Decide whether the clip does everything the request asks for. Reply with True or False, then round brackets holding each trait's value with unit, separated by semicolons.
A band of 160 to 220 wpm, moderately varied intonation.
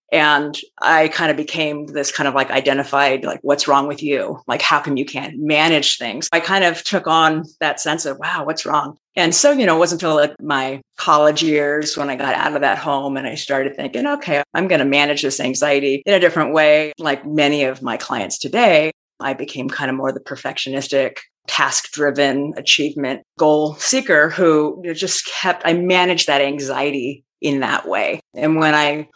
False (200 wpm; 2.2 semitones)